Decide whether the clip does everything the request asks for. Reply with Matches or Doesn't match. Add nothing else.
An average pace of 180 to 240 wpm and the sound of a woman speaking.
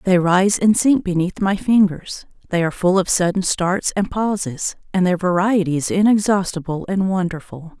Doesn't match